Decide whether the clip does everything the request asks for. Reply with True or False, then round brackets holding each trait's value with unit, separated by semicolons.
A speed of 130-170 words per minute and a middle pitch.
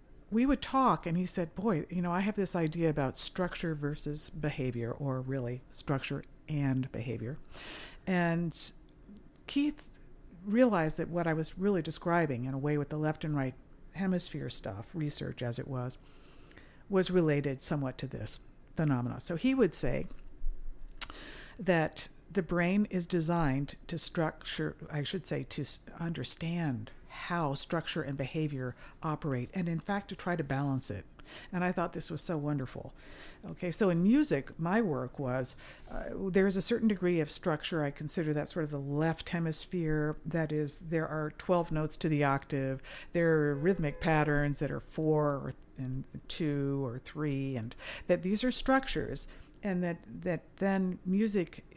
True (165 wpm; 155 Hz)